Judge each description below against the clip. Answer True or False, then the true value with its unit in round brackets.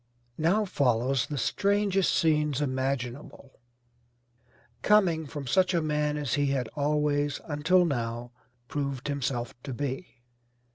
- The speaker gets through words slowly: True (115 wpm)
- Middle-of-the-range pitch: True (145 Hz)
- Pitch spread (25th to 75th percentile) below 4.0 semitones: True (3.2 semitones)